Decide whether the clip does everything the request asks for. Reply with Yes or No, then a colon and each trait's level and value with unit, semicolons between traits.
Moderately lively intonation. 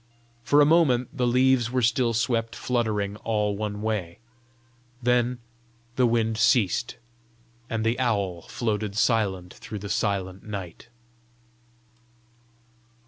Yes: average, 3.1 semitones